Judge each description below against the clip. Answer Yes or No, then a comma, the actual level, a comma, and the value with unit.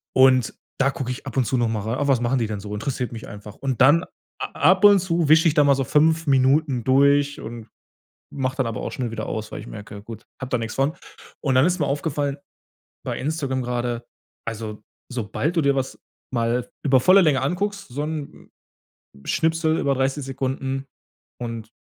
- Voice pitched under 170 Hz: Yes, low, 135 Hz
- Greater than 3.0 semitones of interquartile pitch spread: Yes, average, 3.6 semitones